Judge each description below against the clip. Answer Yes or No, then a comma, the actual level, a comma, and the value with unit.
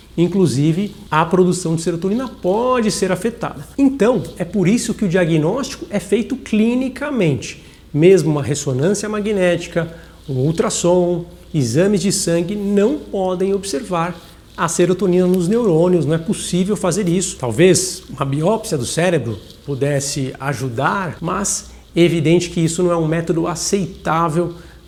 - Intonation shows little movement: No, average, 3.5 semitones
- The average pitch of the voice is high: No, medium, 180 Hz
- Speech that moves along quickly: No, average, 135 wpm